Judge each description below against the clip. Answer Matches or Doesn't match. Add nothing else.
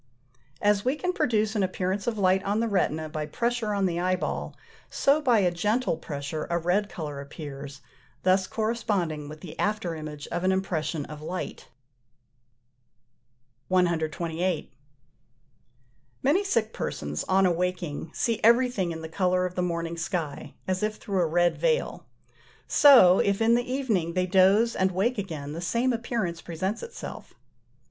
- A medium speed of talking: Matches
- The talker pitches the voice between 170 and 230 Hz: Matches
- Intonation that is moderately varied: Matches